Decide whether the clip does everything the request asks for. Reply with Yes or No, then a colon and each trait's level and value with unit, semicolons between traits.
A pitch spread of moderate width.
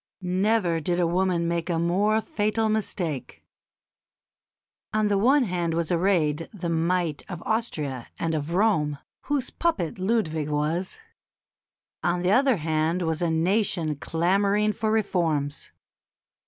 Yes: average, 4.4 semitones